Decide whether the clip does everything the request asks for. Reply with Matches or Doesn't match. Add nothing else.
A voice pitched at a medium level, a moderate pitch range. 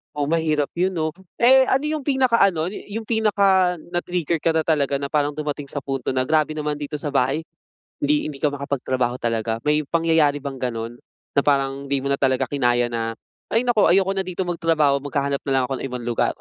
Matches